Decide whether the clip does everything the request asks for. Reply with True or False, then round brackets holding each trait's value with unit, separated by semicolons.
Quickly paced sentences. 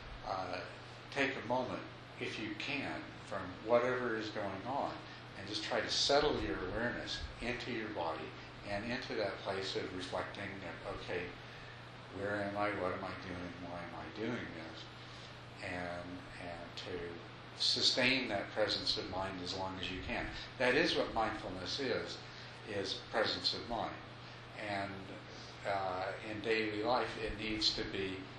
False (155 wpm)